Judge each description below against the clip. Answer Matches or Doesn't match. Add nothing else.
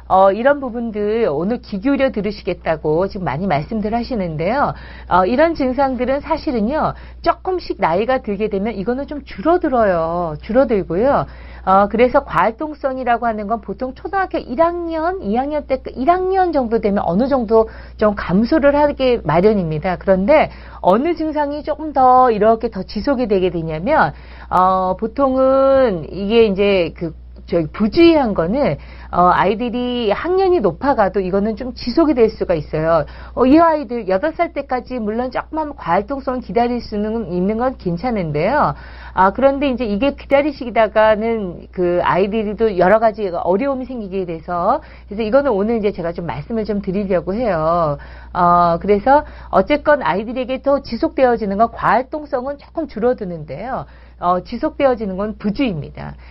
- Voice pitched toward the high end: Matches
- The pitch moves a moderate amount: Doesn't match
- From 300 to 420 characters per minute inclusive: Matches